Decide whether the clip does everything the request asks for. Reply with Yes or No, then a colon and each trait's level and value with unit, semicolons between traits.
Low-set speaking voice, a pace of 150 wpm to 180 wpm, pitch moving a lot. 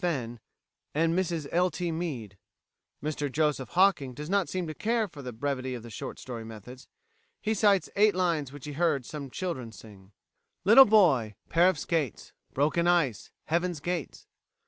No: medium, 155 Hz; average, 165 wpm; wide, 5.7 semitones